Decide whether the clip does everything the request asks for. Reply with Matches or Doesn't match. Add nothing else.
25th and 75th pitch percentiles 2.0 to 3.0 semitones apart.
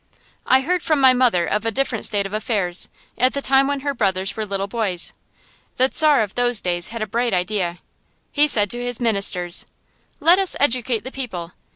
Doesn't match